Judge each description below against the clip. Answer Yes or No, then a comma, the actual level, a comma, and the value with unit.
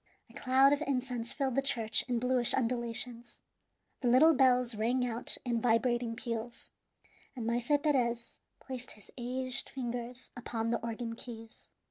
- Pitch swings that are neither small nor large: No, narrow, 1.7 semitones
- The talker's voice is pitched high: Yes, high, 245 Hz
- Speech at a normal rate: Yes, average, 145 wpm